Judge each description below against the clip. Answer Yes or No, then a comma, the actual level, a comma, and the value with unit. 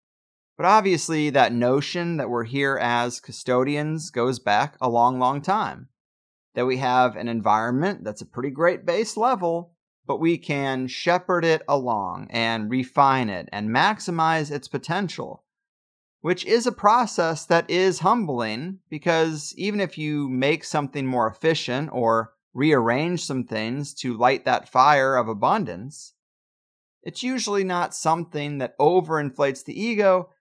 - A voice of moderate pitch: Yes, medium, 145 Hz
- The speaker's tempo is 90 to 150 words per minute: Yes, average, 140 wpm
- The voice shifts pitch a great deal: Yes, wide, 5.7 semitones